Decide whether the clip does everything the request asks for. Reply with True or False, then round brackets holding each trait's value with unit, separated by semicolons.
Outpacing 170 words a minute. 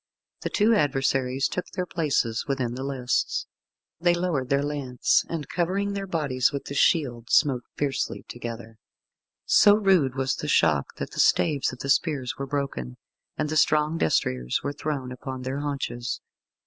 False (160 wpm)